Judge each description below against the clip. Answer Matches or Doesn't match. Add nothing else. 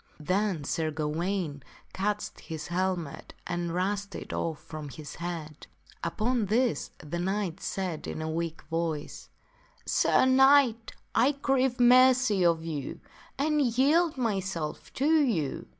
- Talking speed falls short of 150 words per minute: Matches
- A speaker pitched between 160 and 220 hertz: Matches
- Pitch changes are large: Matches